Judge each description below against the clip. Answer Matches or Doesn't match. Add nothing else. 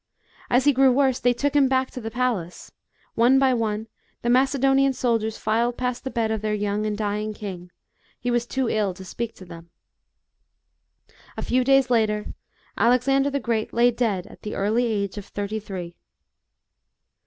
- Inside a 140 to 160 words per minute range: Doesn't match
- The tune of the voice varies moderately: Matches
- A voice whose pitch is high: Matches